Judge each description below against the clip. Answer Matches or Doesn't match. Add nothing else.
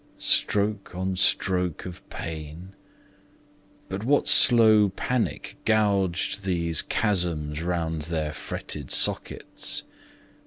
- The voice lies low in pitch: Matches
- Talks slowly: Matches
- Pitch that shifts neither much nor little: Matches